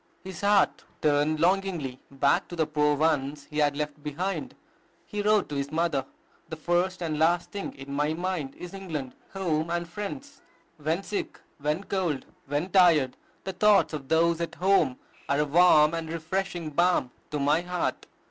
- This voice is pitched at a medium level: Yes, medium, 160 Hz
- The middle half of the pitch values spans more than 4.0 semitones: No, average, 3.7 semitones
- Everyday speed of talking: Yes, average, 170 wpm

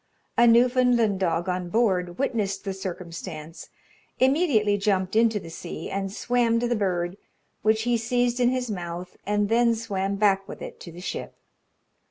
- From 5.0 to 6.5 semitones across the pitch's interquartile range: No, average, 4.3 semitones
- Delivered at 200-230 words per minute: No, average, 165 wpm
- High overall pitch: Yes, high, 205 Hz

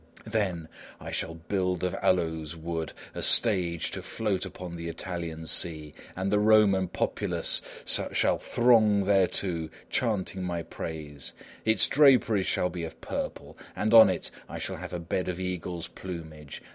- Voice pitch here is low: Yes, very low, 90 Hz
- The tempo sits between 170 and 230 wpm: No, average, 150 wpm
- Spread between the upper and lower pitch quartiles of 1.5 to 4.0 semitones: Yes, average, 3.4 semitones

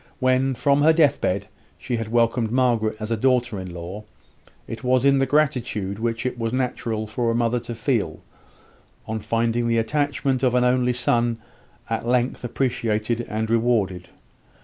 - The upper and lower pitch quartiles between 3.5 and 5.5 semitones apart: No, narrow, 2.5 semitones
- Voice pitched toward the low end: Yes, low, 120 Hz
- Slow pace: No, average, 165 wpm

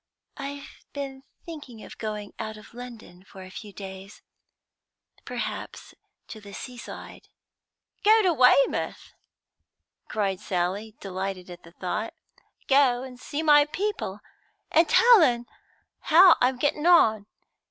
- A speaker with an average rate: No, slow, 125 wpm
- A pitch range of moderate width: No, wide, 6.5 semitones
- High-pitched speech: Yes, high, 240 Hz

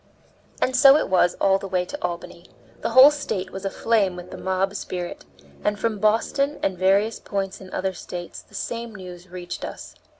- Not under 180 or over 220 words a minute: Yes, average, 190 wpm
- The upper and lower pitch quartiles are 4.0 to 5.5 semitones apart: No, average, 3.6 semitones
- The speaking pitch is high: Yes, high, 195 Hz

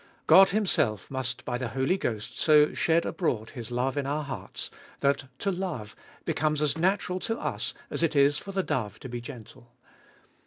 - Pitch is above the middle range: No, medium, 140 Hz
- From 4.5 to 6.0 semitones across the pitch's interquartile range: Yes, wide, 5.6 semitones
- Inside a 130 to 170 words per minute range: No, average, 185 wpm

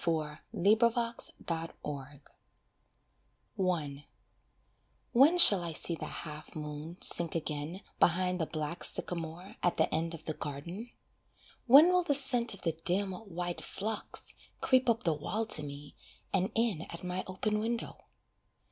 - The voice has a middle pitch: Yes, medium, 175 Hz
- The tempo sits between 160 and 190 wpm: No, average, 145 wpm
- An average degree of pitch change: No, wide, 5.8 semitones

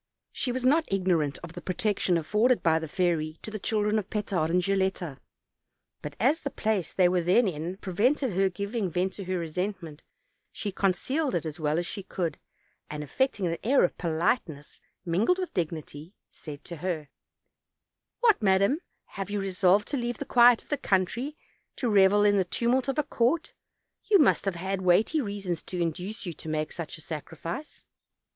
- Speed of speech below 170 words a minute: No, average, 185 wpm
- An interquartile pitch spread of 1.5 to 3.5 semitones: No, average, 4.7 semitones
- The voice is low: No, high, 190 Hz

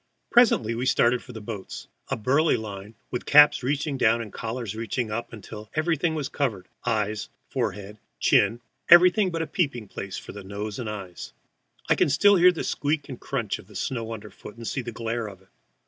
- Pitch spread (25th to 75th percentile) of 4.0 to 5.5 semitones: Yes, average, 5.0 semitones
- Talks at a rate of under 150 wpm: No, average, 195 wpm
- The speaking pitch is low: Yes, low, 115 Hz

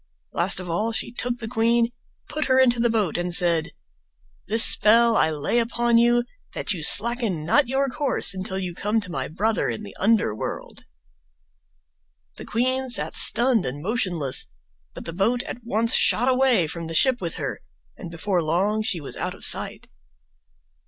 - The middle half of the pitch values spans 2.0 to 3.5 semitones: No, wide, 5.4 semitones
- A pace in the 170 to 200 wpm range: Yes, average, 180 wpm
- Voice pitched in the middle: No, high, 220 Hz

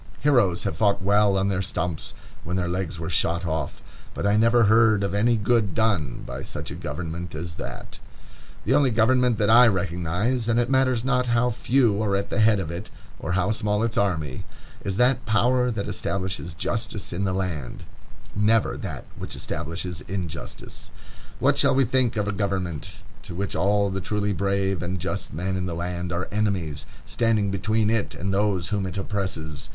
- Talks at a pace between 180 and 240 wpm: Yes, average, 185 wpm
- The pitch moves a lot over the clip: No, average, 3.8 semitones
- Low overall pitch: Yes, low, 100 Hz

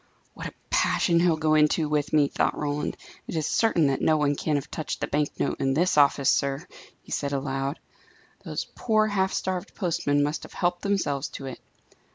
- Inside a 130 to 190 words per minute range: No, average, 200 wpm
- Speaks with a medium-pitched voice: Yes, medium, 150 Hz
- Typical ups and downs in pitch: Yes, average, 3.4 semitones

